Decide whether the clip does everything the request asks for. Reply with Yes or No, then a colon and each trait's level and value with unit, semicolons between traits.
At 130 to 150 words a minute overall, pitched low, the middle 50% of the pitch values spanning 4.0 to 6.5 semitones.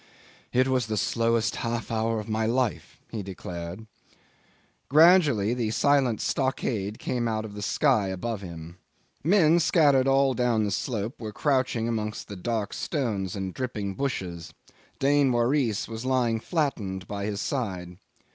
Yes: average, 145 wpm; low, 115 Hz; average, 4.3 semitones